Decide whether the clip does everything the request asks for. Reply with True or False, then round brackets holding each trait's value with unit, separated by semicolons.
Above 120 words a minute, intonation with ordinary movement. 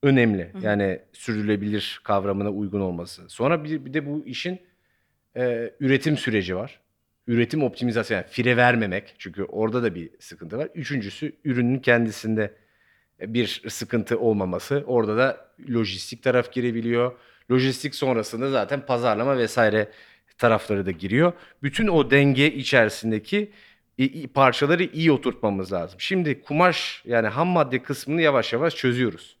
True (130 wpm; 4.6 semitones)